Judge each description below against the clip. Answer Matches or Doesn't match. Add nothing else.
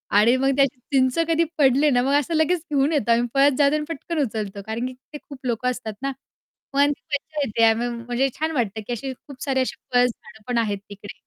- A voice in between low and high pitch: Doesn't match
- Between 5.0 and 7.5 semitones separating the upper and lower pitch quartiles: Doesn't match